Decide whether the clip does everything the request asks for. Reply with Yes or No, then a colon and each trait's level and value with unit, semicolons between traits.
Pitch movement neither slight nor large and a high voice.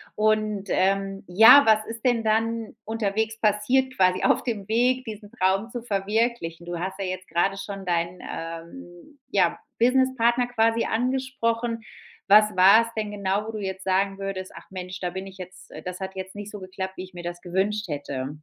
Yes: average, 3.4 semitones; high, 200 Hz